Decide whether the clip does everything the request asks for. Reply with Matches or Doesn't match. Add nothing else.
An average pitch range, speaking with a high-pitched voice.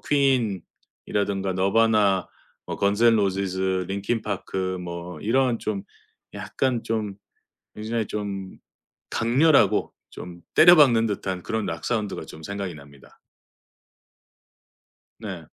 Doesn't match